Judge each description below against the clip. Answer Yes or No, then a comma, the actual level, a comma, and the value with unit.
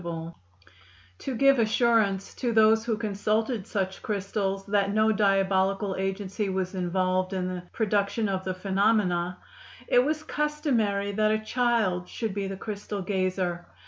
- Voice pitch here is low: No, high, 200 Hz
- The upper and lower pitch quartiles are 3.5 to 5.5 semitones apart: No, narrow, 2.6 semitones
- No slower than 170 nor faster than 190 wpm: No, average, 145 wpm